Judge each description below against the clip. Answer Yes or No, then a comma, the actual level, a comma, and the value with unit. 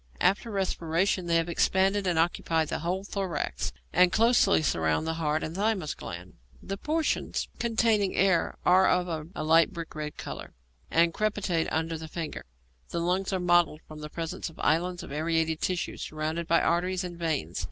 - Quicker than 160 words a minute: Yes, average, 170 wpm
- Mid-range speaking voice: Yes, medium, 170 Hz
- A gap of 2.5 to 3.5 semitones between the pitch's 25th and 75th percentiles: Yes, average, 2.9 semitones